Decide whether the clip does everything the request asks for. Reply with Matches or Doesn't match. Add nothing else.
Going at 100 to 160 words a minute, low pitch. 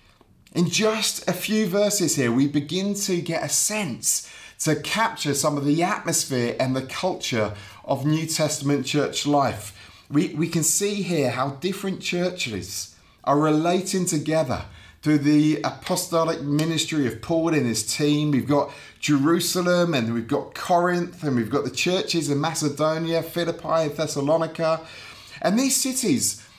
Doesn't match